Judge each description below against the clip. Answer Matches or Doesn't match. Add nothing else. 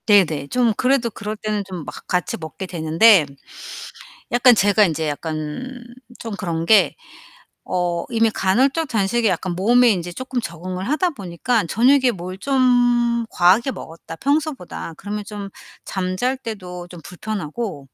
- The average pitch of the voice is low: Doesn't match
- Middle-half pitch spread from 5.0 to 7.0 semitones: Matches